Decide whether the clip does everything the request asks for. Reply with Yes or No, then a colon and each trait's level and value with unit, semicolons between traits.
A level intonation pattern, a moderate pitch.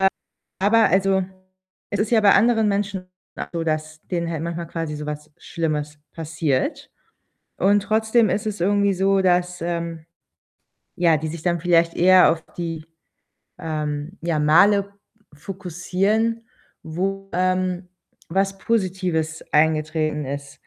No: average, 3.6 semitones; medium, 175 Hz